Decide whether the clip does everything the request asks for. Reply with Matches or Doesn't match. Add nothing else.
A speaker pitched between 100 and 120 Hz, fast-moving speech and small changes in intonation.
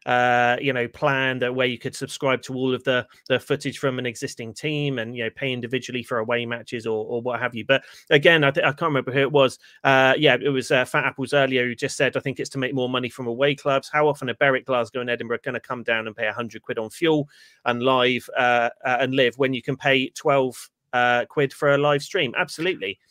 Doesn't match